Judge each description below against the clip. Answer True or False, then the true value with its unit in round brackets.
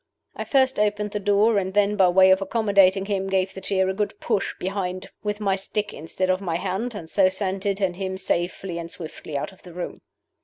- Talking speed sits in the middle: False (225 wpm)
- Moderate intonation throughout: False (1.7 semitones)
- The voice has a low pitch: False (195 Hz)